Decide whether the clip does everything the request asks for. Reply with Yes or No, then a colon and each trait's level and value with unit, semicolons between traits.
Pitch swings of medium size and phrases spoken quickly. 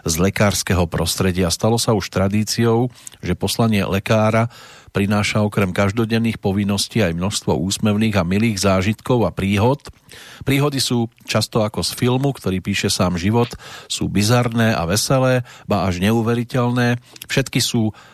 No: average, 3.4 semitones; average, 135 wpm